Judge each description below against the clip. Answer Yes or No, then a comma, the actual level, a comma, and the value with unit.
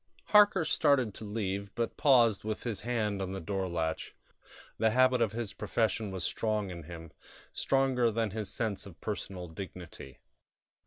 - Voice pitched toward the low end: Yes, low, 105 Hz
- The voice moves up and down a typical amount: Yes, average, 3.7 semitones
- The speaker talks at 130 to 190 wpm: Yes, average, 160 wpm